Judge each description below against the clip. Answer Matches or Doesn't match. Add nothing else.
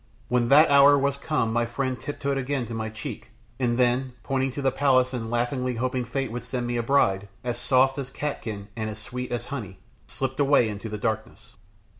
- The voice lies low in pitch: Matches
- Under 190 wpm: Doesn't match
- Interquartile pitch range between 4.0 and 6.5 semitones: Doesn't match